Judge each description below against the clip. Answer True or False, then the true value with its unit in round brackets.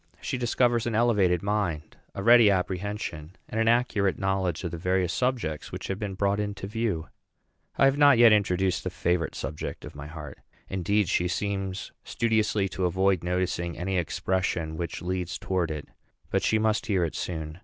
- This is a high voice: False (95 Hz)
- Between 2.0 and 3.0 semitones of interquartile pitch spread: False (3.4 semitones)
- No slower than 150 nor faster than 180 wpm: True (175 wpm)